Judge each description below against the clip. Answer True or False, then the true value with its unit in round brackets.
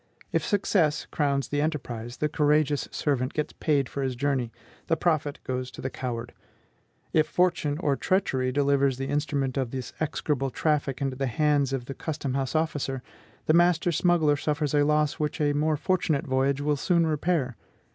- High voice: False (145 Hz)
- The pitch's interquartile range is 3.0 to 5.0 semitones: False (2.5 semitones)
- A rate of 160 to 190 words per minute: True (175 wpm)